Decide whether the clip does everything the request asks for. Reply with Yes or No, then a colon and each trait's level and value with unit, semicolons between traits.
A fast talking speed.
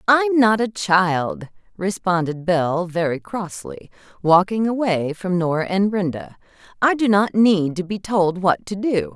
No: average, 155 wpm